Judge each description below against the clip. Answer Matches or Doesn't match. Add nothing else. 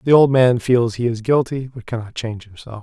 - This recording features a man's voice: Matches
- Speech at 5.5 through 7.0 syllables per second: Matches